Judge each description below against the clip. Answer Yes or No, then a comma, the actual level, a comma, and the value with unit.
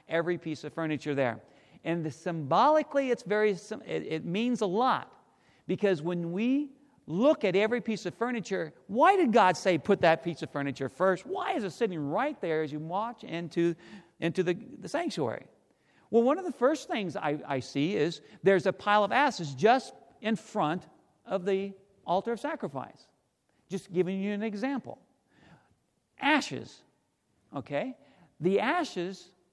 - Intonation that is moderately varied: No, wide, 5.8 semitones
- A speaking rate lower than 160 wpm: No, average, 165 wpm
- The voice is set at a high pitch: Yes, high, 195 Hz